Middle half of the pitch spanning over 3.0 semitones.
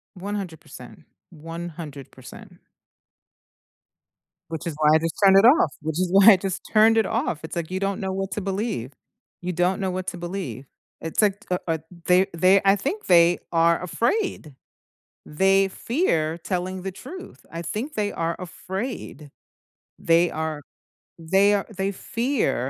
Yes: average, 3.5 semitones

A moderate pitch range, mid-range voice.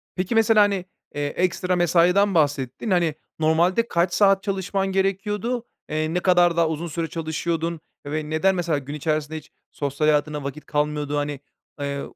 Yes: average, 3.9 semitones; medium, 165 Hz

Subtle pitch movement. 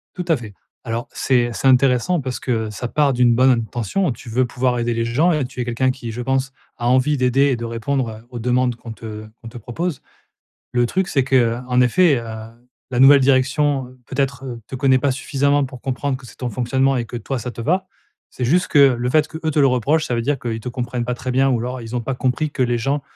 Yes: narrow, 2.3 semitones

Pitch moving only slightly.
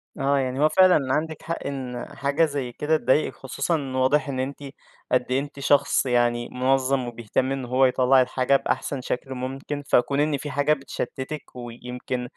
Yes: narrow, 2.1 semitones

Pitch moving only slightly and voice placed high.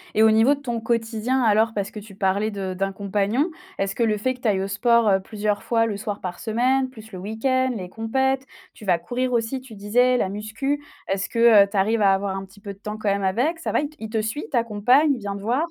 No: average, 3.5 semitones; high, 220 Hz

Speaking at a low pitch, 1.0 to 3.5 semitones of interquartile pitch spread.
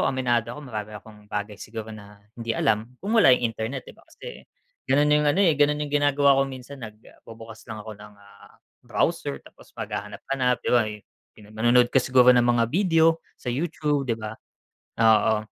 No: low, 120 Hz; average, 4.5 semitones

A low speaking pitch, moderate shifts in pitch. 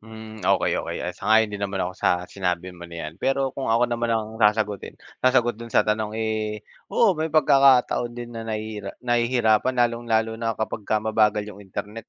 No: low, 110 Hz; narrow, 2.2 semitones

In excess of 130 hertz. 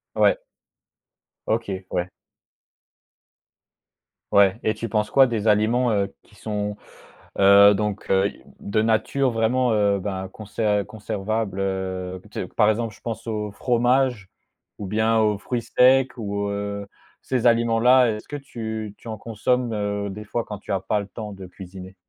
No: low, 105 Hz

